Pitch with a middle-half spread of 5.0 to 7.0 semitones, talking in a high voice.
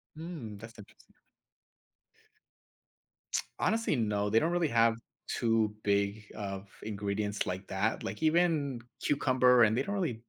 No: wide, 5.6 semitones; low, 115 Hz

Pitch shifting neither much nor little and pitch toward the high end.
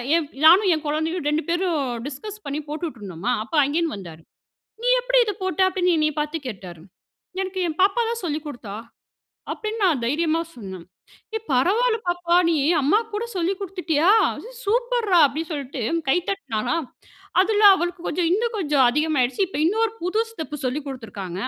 No: wide, 5.8 semitones; very high, 330 Hz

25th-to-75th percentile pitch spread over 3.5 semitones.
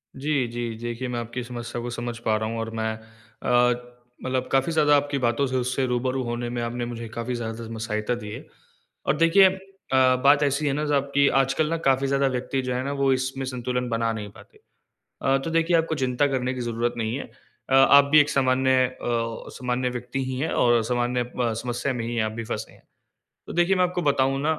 No: narrow, 2.5 semitones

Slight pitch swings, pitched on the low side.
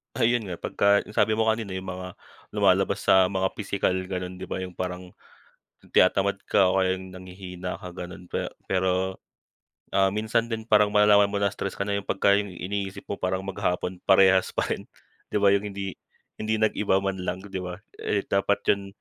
Yes: narrow, 1.6 semitones; very low, 95 Hz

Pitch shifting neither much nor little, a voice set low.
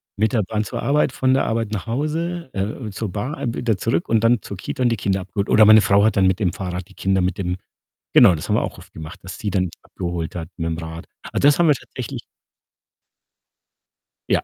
Yes: average, 4.5 semitones; low, 105 Hz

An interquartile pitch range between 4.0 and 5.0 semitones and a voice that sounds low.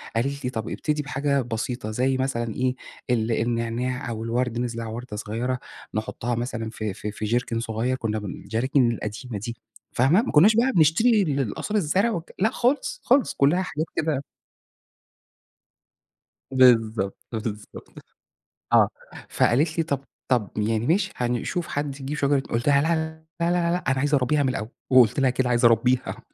Yes: average, 4.4 semitones; low, 125 Hz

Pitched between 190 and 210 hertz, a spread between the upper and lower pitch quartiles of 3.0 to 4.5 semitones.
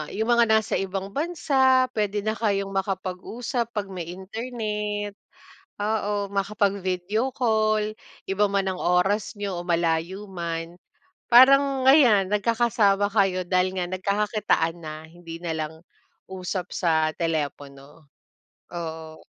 Yes: high, 195 Hz; average, 3.6 semitones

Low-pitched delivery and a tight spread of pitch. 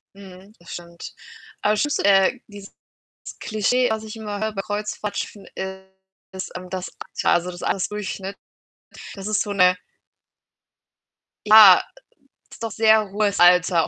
No: high, 200 Hz; narrow, 2.1 semitones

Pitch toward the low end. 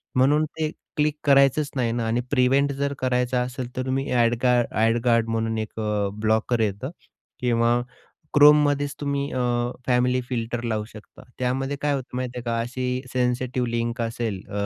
Yes: low, 125 Hz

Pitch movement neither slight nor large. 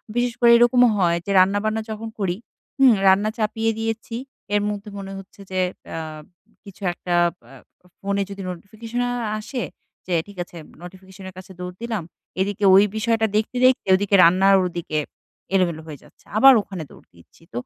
Yes: average, 3.4 semitones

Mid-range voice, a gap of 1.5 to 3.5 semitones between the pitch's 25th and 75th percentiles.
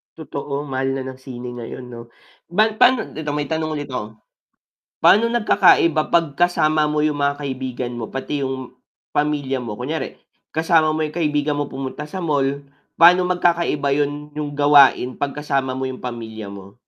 Yes: medium, 145 Hz; average, 2.9 semitones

